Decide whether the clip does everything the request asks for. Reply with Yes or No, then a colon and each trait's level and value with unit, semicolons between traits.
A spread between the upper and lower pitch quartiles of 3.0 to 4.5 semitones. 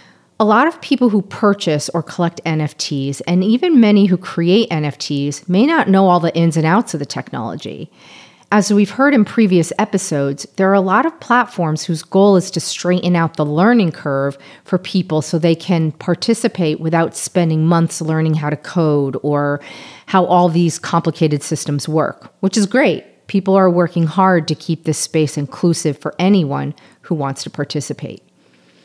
Yes: average, 4.2 semitones